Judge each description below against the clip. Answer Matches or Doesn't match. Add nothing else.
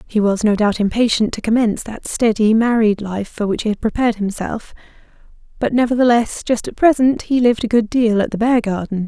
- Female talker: Matches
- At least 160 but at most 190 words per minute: Doesn't match